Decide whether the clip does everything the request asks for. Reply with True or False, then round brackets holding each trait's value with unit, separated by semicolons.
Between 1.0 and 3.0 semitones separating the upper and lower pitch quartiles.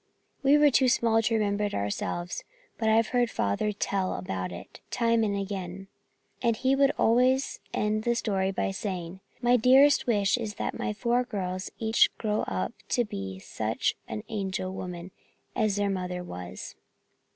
False (4.3 semitones)